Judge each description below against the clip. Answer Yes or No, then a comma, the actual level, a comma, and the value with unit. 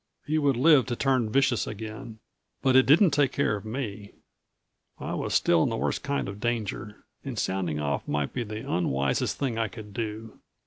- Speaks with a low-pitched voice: Yes, low, 115 Hz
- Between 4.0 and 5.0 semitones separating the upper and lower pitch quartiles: Yes, average, 4.5 semitones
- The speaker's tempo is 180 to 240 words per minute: Yes, average, 190 wpm